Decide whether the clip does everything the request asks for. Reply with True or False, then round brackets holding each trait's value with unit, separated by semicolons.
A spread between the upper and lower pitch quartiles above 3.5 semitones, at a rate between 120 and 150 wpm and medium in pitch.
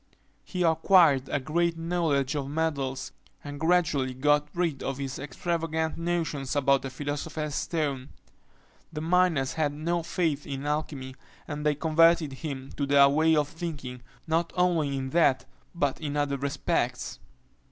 False (2.9 semitones; 145 wpm; 150 Hz)